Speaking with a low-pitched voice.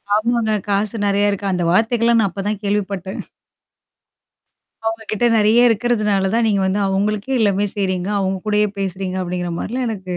No: high, 205 Hz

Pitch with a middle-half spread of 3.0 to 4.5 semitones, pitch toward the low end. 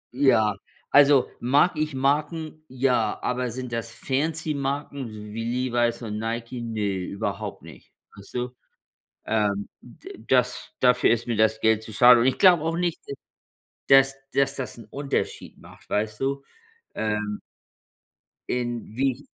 Yes: average, 3.7 semitones; low, 125 Hz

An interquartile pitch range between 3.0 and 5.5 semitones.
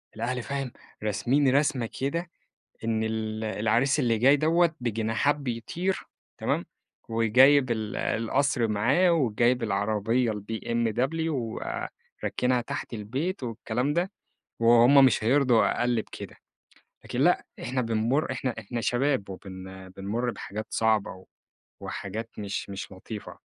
Yes: average, 3.7 semitones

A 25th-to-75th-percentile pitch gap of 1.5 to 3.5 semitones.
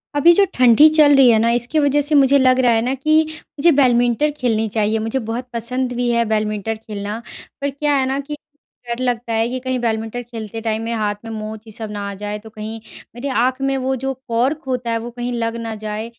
Yes: average, 2.9 semitones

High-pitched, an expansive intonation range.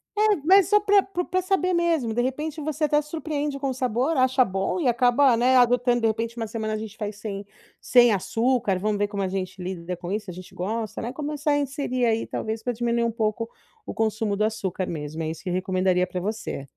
Yes: high, 230 Hz; wide, 5.8 semitones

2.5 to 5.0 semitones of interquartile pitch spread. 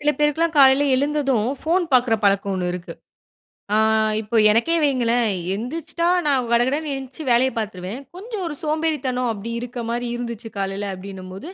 No: wide, 5.6 semitones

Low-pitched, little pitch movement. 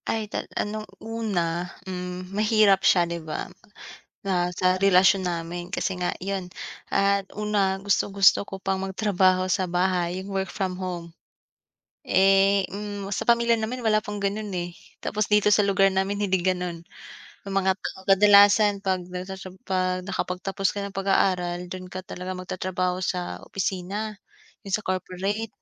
No: high, 190 Hz; narrow, 1.7 semitones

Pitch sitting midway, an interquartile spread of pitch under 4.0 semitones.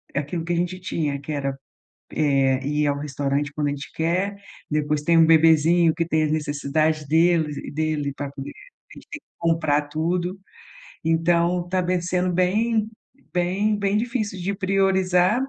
Yes: medium, 165 Hz; average, 3.6 semitones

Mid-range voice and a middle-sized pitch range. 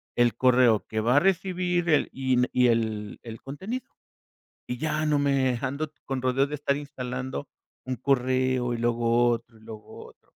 No: low, 130 Hz; average, 3.2 semitones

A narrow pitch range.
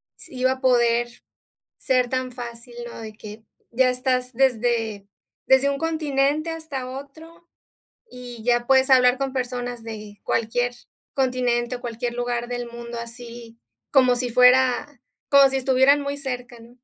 Yes: narrow, 1.8 semitones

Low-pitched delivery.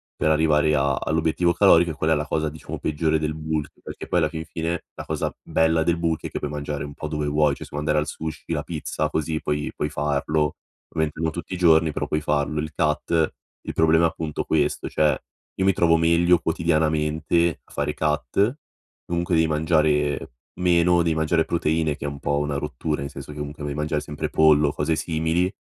Yes: very low, 80 Hz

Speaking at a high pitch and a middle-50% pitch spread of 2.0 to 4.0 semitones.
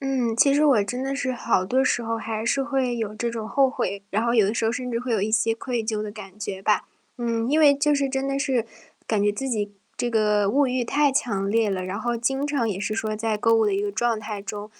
Yes: high, 230 Hz; average, 3.6 semitones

